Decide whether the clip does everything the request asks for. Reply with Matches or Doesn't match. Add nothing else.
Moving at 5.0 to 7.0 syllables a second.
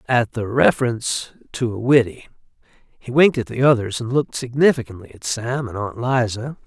Matches